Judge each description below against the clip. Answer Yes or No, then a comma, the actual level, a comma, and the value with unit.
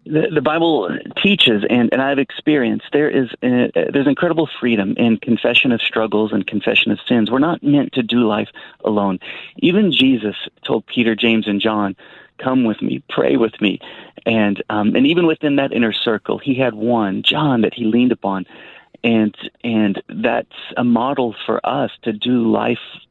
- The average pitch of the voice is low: Yes, low, 120 Hz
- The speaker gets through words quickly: No, average, 175 wpm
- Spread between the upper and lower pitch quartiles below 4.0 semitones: No, average, 4.3 semitones